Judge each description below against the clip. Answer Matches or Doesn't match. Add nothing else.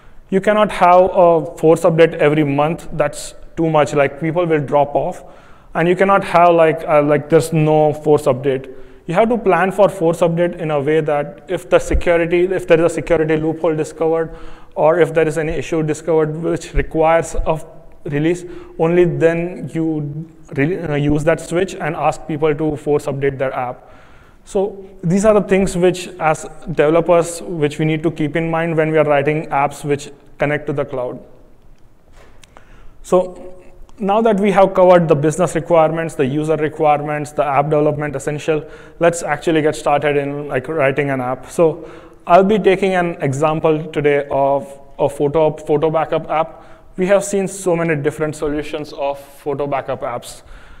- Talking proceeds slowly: Doesn't match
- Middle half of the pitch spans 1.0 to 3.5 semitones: Matches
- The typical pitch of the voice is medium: Matches